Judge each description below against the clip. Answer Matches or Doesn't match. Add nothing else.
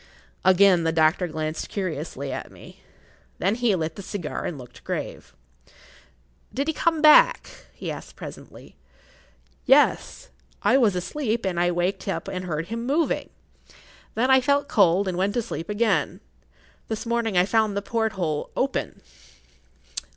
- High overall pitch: Matches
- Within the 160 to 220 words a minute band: Doesn't match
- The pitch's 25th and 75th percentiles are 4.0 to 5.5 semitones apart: Matches